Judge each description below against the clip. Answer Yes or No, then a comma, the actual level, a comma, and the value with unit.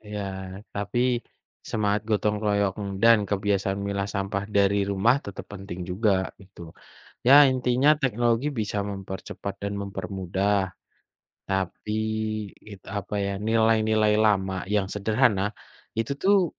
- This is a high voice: No, low, 100 Hz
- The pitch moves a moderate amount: No, narrow, 2.2 semitones